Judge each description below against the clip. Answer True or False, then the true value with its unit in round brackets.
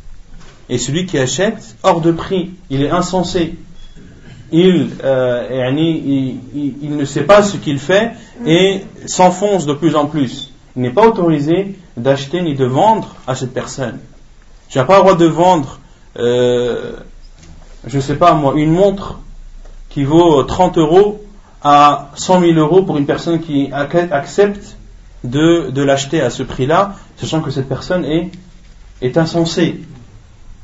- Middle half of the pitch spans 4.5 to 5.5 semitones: True (5.1 semitones)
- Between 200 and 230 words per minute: False (155 wpm)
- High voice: False (155 Hz)